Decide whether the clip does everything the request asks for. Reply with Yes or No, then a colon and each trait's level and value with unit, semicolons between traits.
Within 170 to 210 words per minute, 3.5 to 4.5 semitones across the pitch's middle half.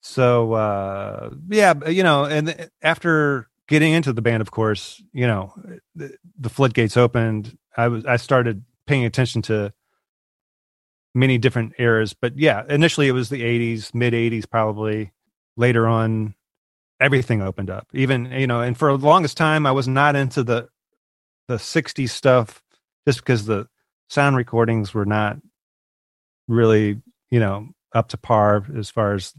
No: average, 155 wpm; average, 4.0 semitones